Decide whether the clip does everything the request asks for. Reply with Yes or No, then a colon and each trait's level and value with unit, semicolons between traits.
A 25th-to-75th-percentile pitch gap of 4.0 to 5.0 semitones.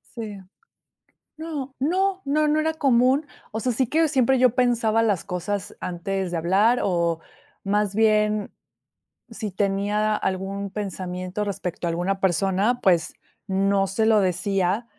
Yes: average, 4.4 semitones